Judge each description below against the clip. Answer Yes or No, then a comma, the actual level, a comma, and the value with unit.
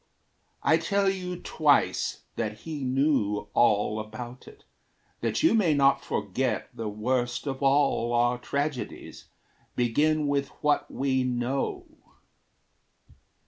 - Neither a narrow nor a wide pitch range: Yes, average, 3.8 semitones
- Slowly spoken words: Yes, slow, 115 wpm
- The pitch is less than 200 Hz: Yes, low, 135 Hz